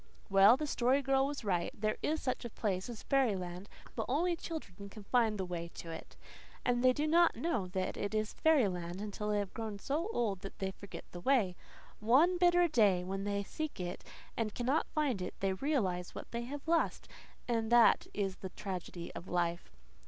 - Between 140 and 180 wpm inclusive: No, average, 195 wpm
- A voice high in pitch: Yes, high, 215 Hz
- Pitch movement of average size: No, wide, 6.2 semitones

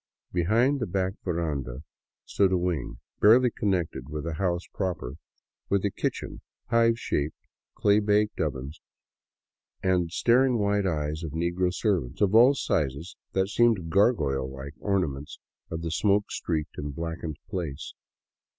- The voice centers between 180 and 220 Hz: No, very low, 90 Hz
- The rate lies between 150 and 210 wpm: No, average, 140 wpm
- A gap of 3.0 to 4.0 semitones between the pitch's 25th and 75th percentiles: No, average, 5.0 semitones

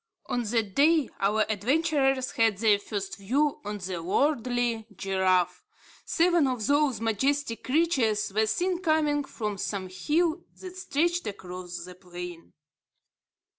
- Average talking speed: No, slow, 130 wpm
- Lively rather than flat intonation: Yes, wide, 7.0 semitones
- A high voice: Yes, high, 230 Hz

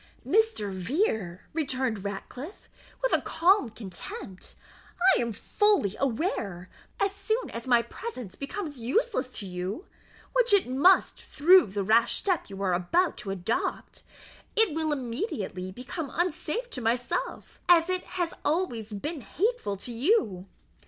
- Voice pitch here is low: No, very high, 255 Hz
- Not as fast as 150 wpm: Yes, average, 140 wpm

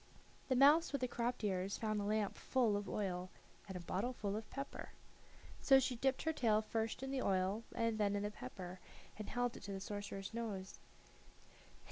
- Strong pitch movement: No, average, 3.7 semitones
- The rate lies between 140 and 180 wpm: No, average, 195 wpm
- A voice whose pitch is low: No, high, 215 Hz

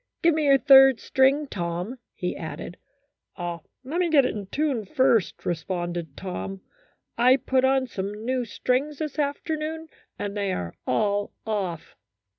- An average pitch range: No, wide, 6.7 semitones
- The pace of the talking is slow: No, average, 150 wpm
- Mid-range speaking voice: No, high, 235 Hz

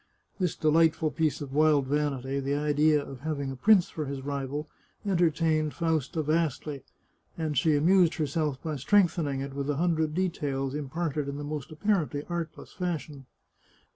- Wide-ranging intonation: No, narrow, 2.6 semitones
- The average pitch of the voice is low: No, medium, 150 Hz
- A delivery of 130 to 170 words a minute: Yes, average, 155 wpm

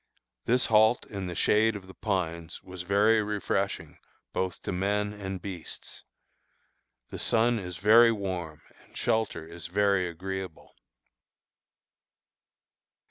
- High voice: No, very low, 95 Hz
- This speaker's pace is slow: Yes, slow, 120 wpm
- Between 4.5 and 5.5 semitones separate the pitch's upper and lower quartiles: No, average, 2.9 semitones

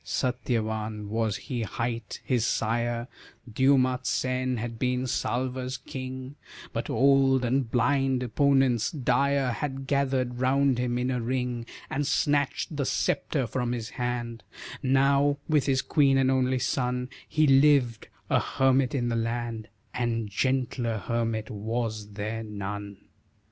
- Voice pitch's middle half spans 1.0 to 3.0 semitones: Yes, narrow, 2.5 semitones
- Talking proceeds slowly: Yes, slow, 130 wpm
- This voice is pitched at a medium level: No, low, 125 Hz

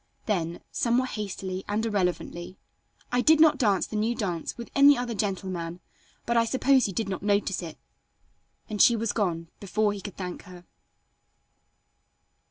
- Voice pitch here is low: No, high, 205 Hz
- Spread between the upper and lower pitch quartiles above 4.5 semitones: No, average, 4.2 semitones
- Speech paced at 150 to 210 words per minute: Yes, average, 160 wpm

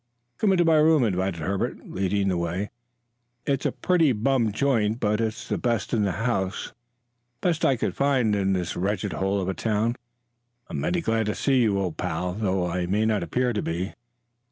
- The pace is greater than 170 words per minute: Yes, average, 200 wpm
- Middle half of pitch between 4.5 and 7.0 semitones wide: Yes, average, 4.8 semitones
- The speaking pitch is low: Yes, low, 105 Hz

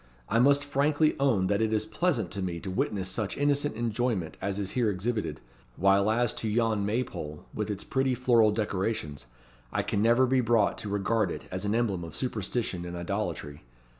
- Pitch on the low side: Yes, low, 110 Hz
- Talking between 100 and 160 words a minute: No, average, 195 wpm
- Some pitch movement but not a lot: Yes, average, 4.0 semitones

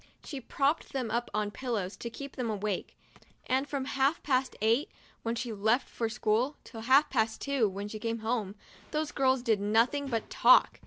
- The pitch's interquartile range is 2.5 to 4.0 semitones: Yes, average, 3.5 semitones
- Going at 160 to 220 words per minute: Yes, average, 190 wpm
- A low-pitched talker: No, high, 235 Hz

